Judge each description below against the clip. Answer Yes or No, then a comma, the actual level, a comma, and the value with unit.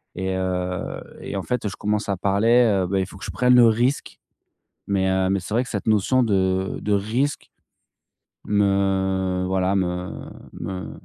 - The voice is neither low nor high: No, very low, 95 Hz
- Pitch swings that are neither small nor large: No, narrow, 2.3 semitones